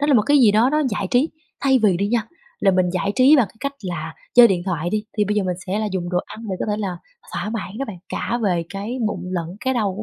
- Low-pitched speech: No, high, 210 Hz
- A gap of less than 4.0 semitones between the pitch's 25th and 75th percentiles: No, average, 4.7 semitones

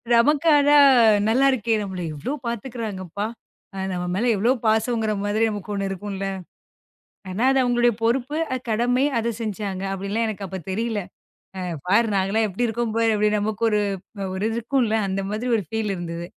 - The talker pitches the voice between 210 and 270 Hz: Yes, high, 220 Hz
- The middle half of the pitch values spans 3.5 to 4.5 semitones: No, average, 3.1 semitones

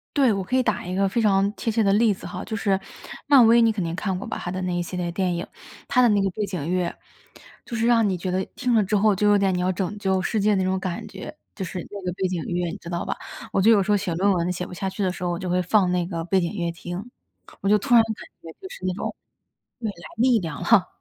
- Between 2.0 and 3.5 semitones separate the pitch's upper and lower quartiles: Yes, average, 2.9 semitones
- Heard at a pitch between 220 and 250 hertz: No, high, 190 Hz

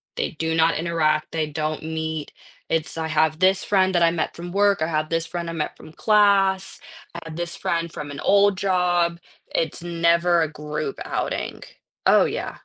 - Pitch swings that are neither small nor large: No, narrow, 2.1 semitones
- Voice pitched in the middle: Yes, medium, 165 Hz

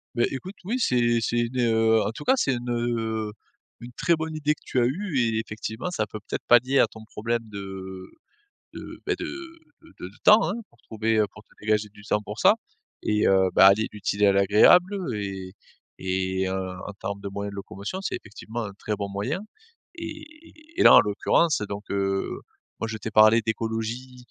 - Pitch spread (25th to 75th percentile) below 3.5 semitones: No, average, 4.2 semitones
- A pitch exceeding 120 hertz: No, low, 110 Hz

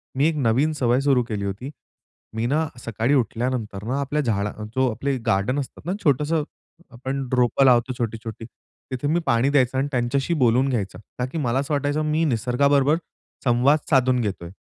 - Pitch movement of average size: Yes, average, 3.2 semitones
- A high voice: No, low, 130 Hz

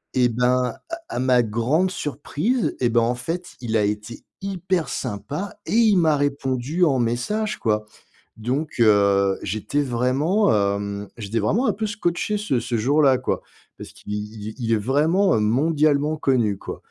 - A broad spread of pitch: Yes, wide, 6.7 semitones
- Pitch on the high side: No, low, 130 Hz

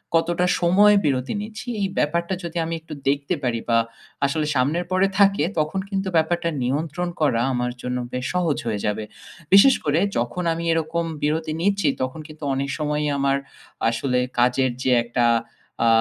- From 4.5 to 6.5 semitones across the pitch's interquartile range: Yes, average, 5.1 semitones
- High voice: No, medium, 155 Hz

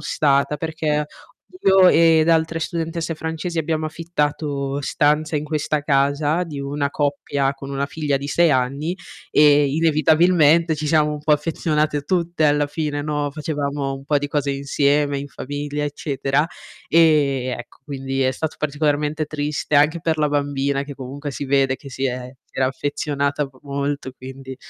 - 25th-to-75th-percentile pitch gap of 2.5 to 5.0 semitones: No, narrow, 1.8 semitones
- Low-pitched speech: No, medium, 145 Hz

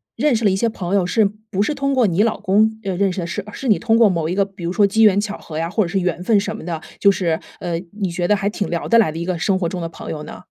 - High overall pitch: Yes, high, 195 Hz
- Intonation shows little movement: No, average, 3.5 semitones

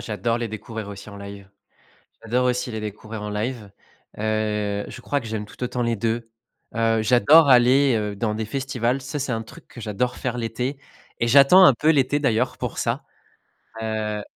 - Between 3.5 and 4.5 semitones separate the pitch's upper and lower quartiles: No, average, 2.9 semitones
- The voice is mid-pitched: No, low, 115 Hz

